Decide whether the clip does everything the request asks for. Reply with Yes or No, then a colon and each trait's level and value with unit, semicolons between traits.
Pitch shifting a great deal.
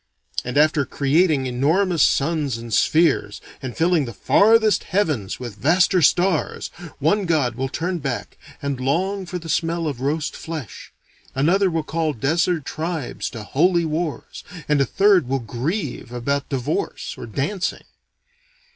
No: average, 4.6 semitones